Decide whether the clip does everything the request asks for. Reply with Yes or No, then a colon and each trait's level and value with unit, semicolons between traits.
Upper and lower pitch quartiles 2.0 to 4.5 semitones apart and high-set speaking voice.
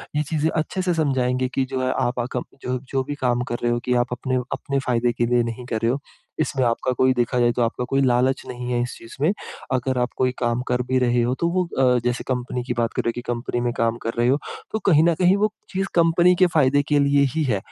No: average, 2.9 semitones; low, 125 Hz